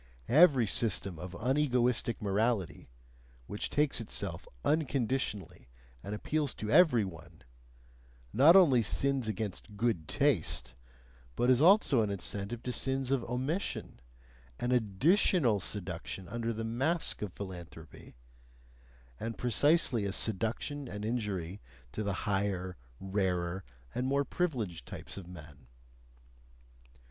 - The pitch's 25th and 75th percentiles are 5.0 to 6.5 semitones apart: Yes, wide, 5.5 semitones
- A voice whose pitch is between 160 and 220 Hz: No, low, 115 Hz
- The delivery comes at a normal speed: No, slow, 115 wpm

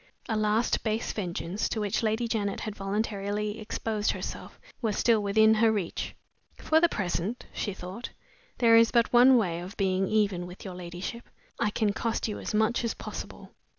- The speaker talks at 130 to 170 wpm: No, average, 180 wpm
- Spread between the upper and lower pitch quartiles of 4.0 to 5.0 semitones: No, narrow, 2.6 semitones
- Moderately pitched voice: No, high, 215 Hz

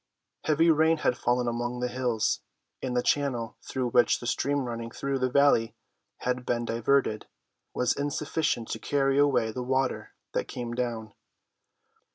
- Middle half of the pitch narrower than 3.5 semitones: Yes, average, 2.8 semitones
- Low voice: Yes, low, 125 Hz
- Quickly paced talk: No, average, 155 wpm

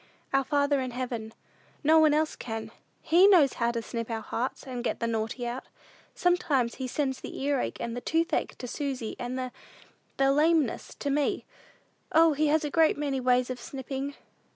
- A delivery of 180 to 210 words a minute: Yes, average, 185 wpm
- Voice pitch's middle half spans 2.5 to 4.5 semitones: Yes, average, 3.4 semitones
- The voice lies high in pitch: Yes, very high, 265 Hz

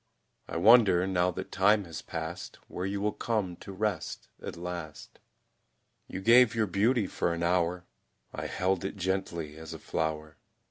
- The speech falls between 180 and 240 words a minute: No, average, 165 wpm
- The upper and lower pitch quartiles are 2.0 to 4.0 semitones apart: Yes, average, 3.1 semitones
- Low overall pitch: Yes, very low, 90 Hz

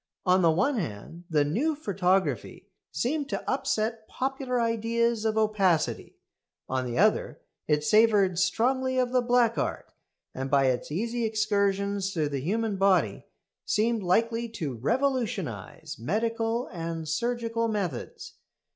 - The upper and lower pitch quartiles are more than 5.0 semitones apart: Yes, wide, 5.6 semitones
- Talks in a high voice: Yes, high, 215 Hz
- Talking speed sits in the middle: No, slow, 130 wpm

